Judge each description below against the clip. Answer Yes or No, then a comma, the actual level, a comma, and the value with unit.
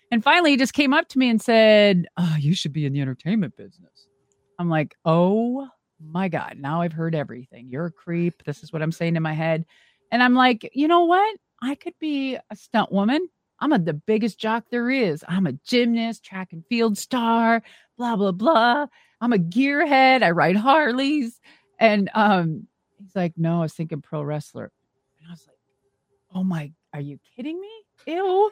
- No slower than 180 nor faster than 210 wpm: Yes, average, 200 wpm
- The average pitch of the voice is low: No, high, 200 Hz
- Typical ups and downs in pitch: No, wide, 7.4 semitones